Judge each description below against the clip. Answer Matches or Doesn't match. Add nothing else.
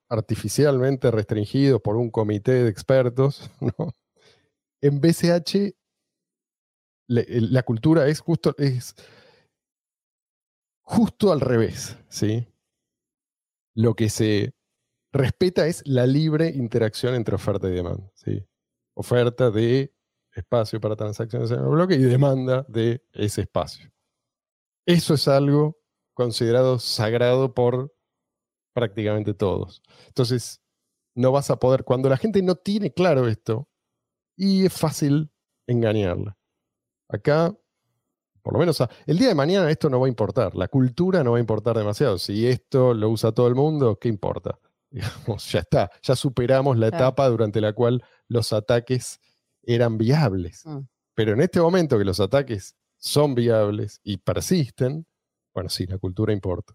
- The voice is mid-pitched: Doesn't match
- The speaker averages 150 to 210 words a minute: Doesn't match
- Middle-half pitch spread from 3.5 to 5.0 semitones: Matches